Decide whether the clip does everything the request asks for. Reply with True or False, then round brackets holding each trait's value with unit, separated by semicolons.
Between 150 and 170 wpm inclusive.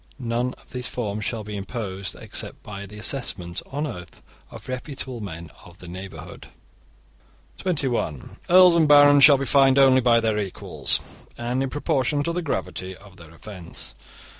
True (165 wpm)